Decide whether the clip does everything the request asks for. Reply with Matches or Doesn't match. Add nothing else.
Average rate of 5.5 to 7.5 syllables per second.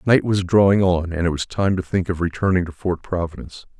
Matches